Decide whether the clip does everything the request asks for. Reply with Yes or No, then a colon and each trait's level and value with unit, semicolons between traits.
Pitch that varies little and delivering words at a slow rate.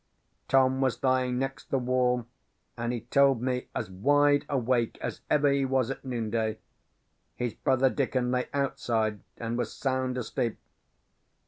No: narrow, 2.2 semitones; average, 145 wpm